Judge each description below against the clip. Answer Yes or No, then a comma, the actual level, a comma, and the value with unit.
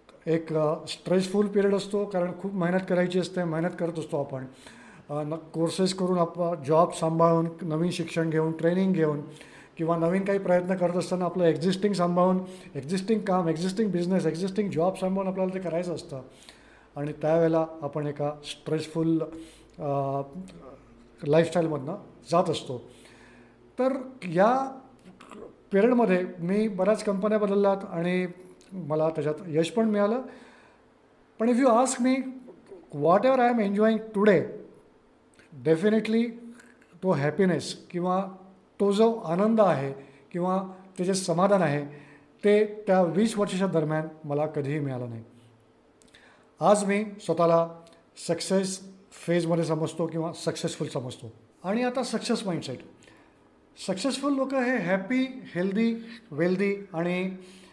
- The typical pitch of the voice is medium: Yes, medium, 175 Hz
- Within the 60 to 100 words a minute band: No, average, 125 wpm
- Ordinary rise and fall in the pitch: Yes, average, 4.1 semitones